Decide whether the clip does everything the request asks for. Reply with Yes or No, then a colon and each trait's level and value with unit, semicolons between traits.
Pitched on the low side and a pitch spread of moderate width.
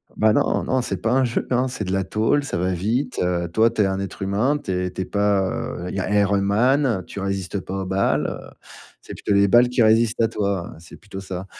Yes: low, 100 Hz; average, 3.3 semitones